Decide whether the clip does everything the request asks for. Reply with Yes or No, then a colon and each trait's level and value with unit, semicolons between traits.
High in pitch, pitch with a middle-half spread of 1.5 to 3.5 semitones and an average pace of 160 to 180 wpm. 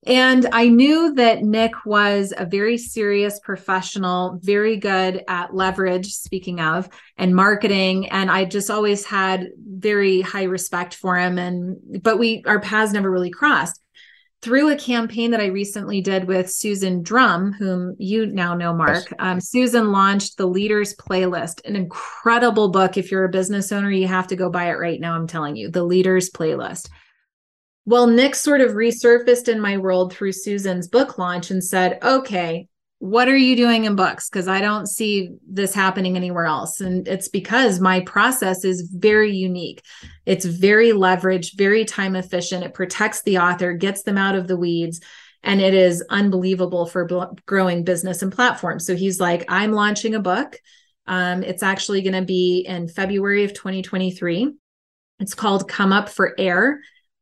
Yes: high, 195 Hz; narrow, 2.5 semitones; average, 175 wpm